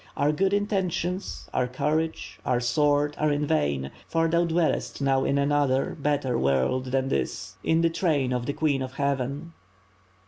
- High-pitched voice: No, medium, 145 Hz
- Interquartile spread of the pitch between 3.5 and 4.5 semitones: Yes, average, 3.9 semitones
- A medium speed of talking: Yes, average, 165 wpm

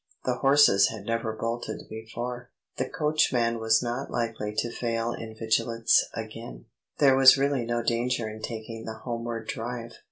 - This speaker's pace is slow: No, average, 155 wpm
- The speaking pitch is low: Yes, low, 115 Hz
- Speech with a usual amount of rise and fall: No, narrow, 1.7 semitones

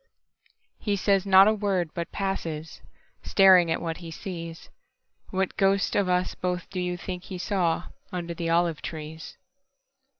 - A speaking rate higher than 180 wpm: No, slow, 135 wpm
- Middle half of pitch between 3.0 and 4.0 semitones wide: No, narrow, 2.5 semitones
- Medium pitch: Yes, medium, 180 Hz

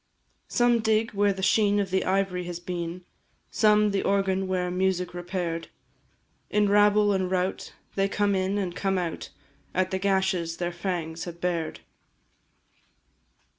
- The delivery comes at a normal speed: Yes, average, 145 wpm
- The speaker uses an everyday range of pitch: No, narrow, 2.1 semitones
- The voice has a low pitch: No, high, 190 Hz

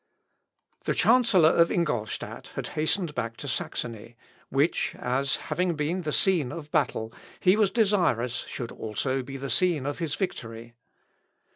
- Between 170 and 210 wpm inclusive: No, average, 150 wpm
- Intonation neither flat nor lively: No, wide, 6.6 semitones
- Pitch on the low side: No, medium, 150 Hz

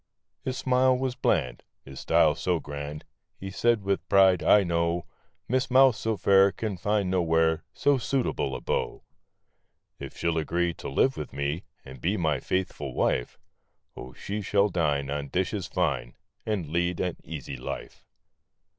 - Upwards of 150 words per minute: Yes, average, 165 wpm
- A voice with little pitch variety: No, wide, 5.6 semitones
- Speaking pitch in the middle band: No, very low, 90 Hz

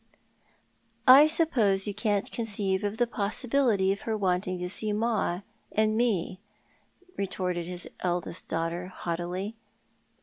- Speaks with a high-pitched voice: Yes, high, 200 Hz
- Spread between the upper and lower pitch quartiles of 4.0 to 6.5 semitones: No, average, 3.4 semitones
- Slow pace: Yes, slow, 125 wpm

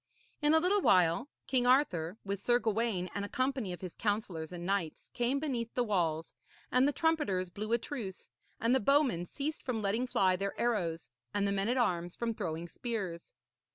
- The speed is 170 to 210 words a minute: Yes, average, 190 wpm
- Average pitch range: No, wide, 5.7 semitones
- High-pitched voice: Yes, high, 210 Hz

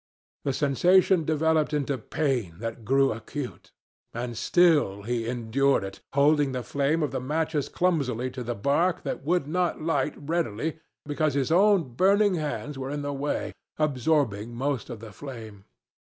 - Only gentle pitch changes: No, average, 4.4 semitones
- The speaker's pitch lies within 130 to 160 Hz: Yes, medium, 140 Hz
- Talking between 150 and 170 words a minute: Yes, average, 155 wpm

